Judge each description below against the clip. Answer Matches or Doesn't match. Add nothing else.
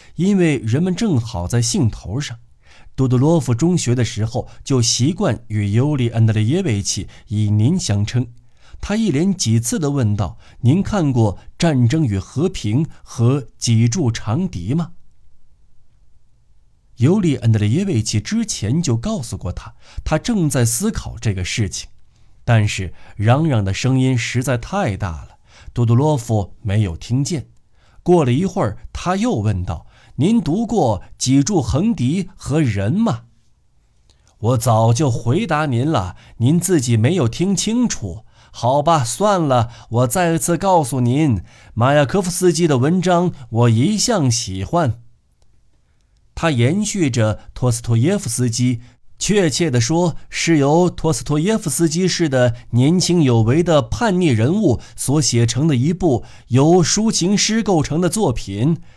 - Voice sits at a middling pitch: Doesn't match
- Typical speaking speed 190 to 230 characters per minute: Matches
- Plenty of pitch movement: Matches